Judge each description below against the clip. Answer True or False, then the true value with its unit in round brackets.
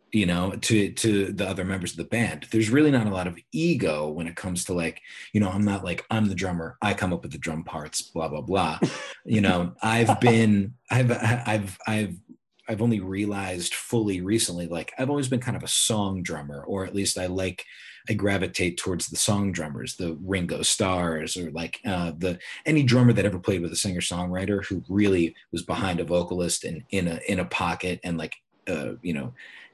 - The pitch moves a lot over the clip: False (3.8 semitones)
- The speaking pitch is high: False (95 Hz)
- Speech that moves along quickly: True (210 wpm)